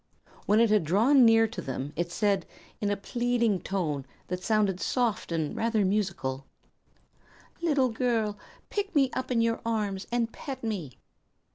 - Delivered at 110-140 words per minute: No, average, 155 wpm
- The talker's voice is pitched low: No, high, 215 Hz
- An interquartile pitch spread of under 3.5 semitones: No, average, 4.2 semitones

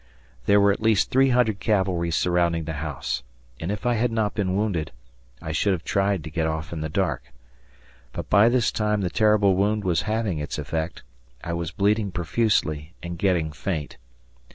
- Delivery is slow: No, average, 185 wpm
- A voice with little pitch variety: No, average, 4.7 semitones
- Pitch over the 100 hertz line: No, very low, 95 Hz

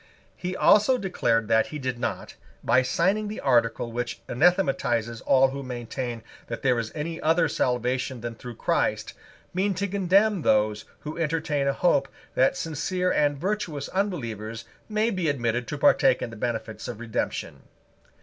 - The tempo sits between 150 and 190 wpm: Yes, average, 160 wpm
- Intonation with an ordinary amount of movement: No, wide, 7.0 semitones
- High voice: No, low, 135 Hz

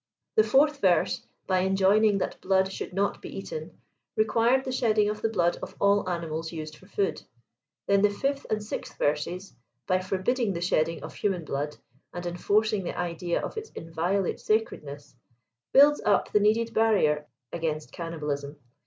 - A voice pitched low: No, high, 190 Hz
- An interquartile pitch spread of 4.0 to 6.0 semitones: Yes, average, 4.5 semitones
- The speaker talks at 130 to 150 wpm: No, average, 160 wpm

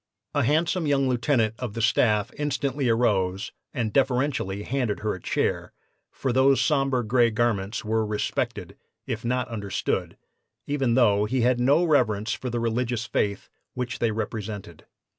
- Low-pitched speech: Yes, low, 120 Hz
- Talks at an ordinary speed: Yes, average, 150 wpm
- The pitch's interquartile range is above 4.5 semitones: No, average, 3.5 semitones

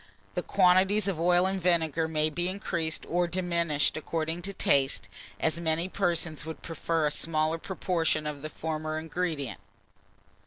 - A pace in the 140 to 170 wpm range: Yes, average, 150 wpm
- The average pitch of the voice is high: No, medium, 165 Hz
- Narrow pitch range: Yes, narrow, 2.2 semitones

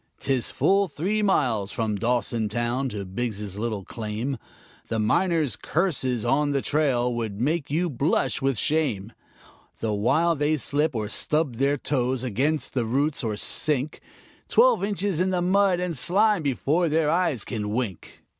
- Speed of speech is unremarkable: Yes, average, 155 wpm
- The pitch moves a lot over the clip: Yes, wide, 5.9 semitones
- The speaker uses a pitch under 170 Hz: Yes, low, 135 Hz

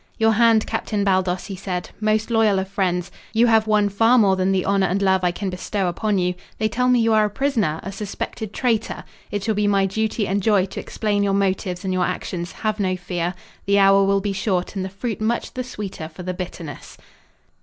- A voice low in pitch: No, high, 200 Hz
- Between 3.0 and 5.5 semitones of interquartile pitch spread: No, narrow, 2.6 semitones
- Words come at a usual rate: No, fast, 225 wpm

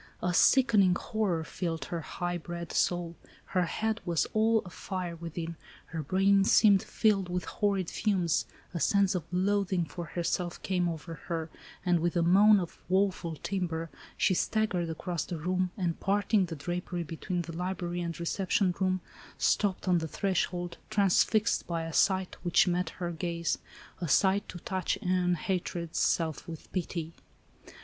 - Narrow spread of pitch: Yes, narrow, 2.2 semitones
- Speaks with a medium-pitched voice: Yes, medium, 180 Hz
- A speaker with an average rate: Yes, average, 155 wpm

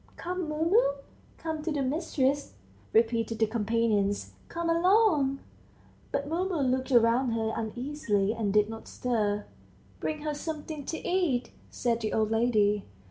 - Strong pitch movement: Yes, wide, 5.7 semitones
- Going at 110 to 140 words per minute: Yes, slow, 135 wpm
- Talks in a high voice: Yes, very high, 255 Hz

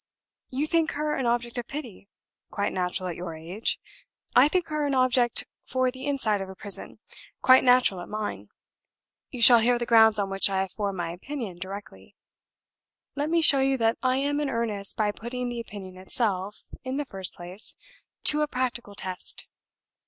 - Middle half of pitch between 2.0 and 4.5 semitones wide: No, average, 5.2 semitones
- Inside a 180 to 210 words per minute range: Yes, average, 185 wpm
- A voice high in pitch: Yes, high, 235 Hz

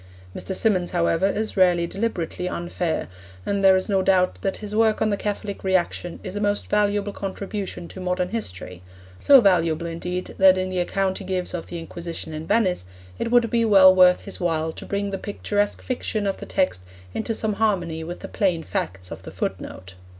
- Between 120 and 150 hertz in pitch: No, high, 190 Hz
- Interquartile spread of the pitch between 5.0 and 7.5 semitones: No, average, 2.8 semitones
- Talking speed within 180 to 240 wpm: Yes, average, 200 wpm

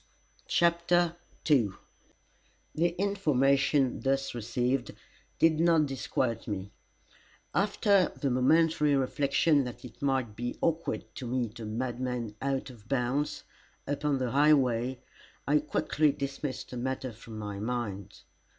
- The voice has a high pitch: No, low, 135 Hz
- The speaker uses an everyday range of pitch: Yes, average, 3.7 semitones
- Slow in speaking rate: Yes, slow, 120 wpm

